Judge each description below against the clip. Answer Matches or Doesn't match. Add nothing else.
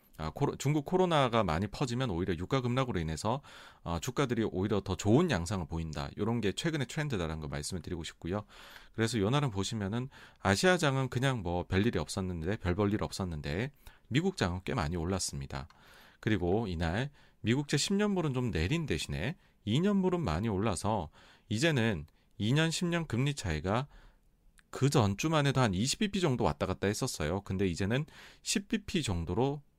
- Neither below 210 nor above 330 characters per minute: Doesn't match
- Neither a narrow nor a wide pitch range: Doesn't match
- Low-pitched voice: Matches